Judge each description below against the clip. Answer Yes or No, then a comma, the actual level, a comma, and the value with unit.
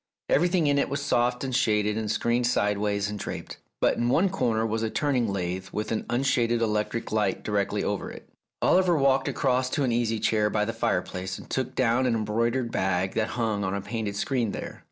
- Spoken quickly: Yes, fast, 210 wpm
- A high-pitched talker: No, low, 115 Hz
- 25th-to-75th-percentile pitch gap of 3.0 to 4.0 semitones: Yes, average, 3.5 semitones